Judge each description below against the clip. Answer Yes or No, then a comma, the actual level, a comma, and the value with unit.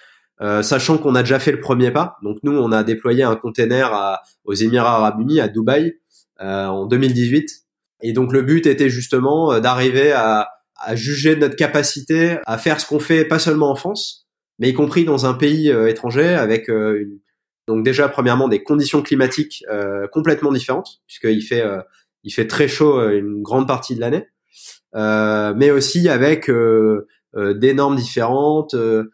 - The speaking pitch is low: Yes, low, 130 Hz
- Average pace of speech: Yes, average, 185 wpm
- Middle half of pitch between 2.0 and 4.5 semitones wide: No, average, 5.0 semitones